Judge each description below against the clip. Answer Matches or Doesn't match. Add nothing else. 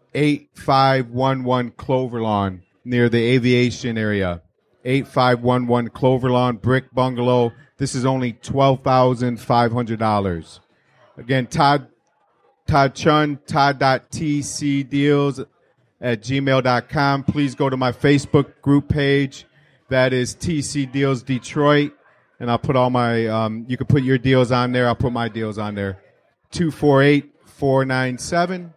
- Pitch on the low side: Matches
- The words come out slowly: Matches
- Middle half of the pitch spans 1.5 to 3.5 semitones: Matches